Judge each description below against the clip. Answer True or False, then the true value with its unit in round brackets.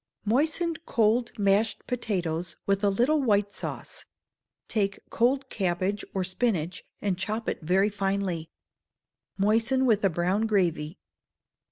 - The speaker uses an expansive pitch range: False (3.5 semitones)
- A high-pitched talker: True (200 Hz)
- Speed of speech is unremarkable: False (125 wpm)